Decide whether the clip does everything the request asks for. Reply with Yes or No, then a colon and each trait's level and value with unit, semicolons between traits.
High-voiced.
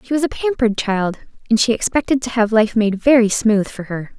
Yes: high, 230 Hz